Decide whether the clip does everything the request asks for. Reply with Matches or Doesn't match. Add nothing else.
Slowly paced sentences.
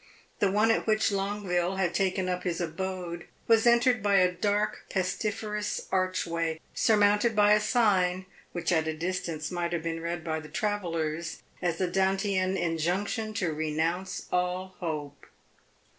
Doesn't match